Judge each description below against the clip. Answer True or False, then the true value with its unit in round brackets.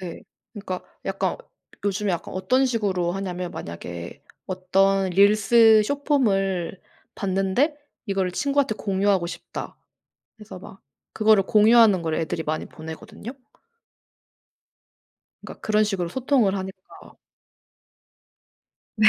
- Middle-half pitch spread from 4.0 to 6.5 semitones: False (3.0 semitones)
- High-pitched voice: True (195 Hz)